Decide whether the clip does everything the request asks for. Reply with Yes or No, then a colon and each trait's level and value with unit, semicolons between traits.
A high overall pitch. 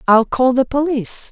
Yes: very high, 260 Hz